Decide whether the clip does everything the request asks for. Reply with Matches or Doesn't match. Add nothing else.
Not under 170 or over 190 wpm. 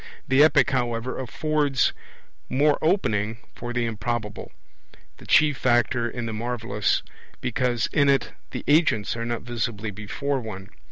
Doesn't match